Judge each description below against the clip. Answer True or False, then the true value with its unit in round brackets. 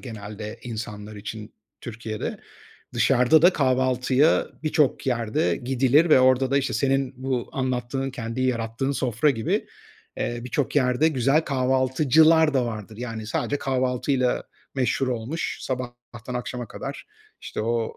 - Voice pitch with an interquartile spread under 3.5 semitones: True (2.5 semitones)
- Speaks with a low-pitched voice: True (125 Hz)